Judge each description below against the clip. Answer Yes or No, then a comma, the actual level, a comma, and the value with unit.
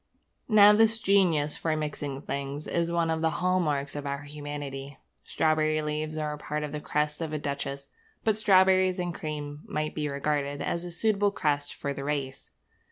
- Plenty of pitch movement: No, average, 3.0 semitones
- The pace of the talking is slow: No, average, 180 wpm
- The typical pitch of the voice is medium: Yes, medium, 150 Hz